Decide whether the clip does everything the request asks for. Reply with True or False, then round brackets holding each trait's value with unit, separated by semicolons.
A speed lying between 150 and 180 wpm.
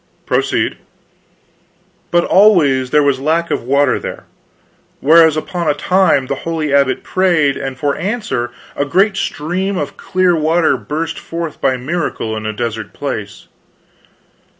False (140 wpm)